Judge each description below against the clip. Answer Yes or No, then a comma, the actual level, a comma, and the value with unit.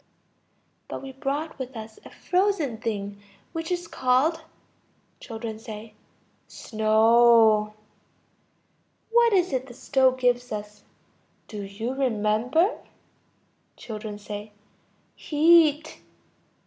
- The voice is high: Yes, very high, 250 Hz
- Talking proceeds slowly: Yes, slow, 90 wpm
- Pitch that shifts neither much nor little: No, wide, 6.1 semitones